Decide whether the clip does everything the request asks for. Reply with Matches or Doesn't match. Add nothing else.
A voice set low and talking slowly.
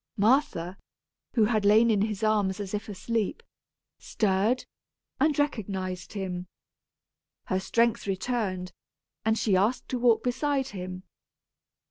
Doesn't match